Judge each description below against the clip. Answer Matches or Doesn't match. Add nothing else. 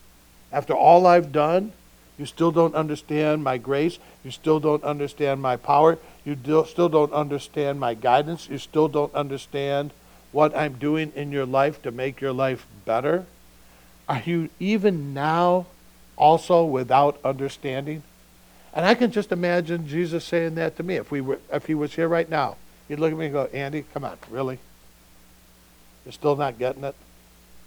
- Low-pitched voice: Doesn't match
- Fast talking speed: Doesn't match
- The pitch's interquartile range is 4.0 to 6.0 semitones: Doesn't match